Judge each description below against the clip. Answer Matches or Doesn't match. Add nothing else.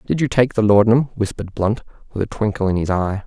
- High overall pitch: Doesn't match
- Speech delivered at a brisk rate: Matches